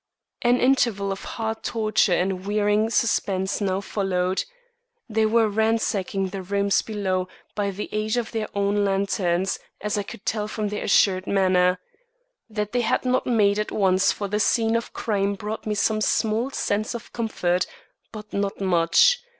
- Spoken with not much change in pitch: Yes, narrow, 2.2 semitones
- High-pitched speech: Yes, high, 205 Hz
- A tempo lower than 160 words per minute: No, average, 165 wpm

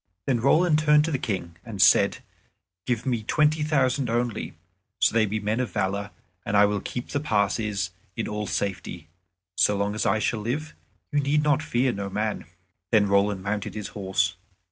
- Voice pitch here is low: Yes, low, 110 Hz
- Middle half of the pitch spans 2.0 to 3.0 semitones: No, average, 4.3 semitones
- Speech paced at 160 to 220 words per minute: Yes, average, 180 wpm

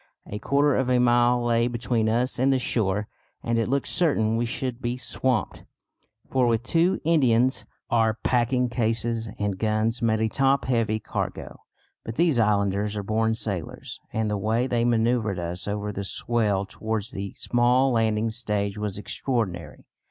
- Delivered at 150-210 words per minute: Yes, average, 165 wpm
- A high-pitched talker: No, low, 115 Hz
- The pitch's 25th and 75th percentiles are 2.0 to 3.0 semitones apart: Yes, narrow, 2.6 semitones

